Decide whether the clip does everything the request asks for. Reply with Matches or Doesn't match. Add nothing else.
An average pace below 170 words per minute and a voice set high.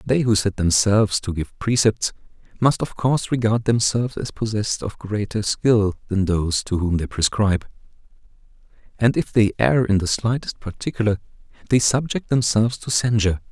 Doesn't match